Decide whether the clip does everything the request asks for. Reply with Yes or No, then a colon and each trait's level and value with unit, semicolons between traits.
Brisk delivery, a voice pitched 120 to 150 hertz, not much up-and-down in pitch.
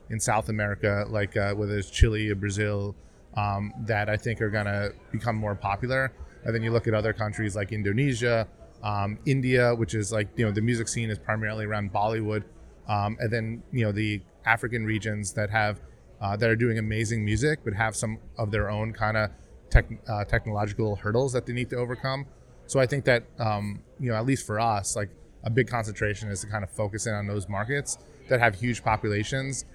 No: fast, 210 wpm; low, 110 Hz; narrow, 2.1 semitones